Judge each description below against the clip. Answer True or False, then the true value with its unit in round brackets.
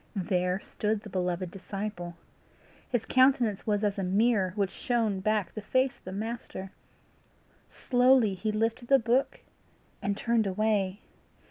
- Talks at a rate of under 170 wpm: True (140 wpm)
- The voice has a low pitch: False (210 Hz)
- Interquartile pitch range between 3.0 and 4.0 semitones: True (3.4 semitones)